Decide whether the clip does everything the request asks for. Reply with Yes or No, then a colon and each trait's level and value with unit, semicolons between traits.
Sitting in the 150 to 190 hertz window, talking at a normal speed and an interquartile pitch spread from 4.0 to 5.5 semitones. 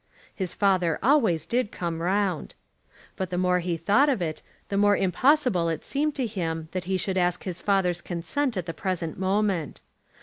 No: medium, 185 Hz; average, 180 wpm; average, 3.2 semitones